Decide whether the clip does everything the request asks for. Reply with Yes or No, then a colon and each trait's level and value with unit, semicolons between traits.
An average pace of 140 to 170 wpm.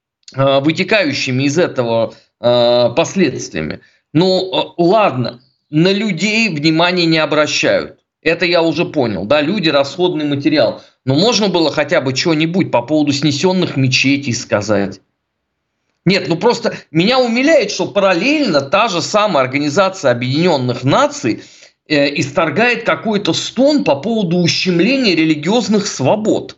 No: average, 115 wpm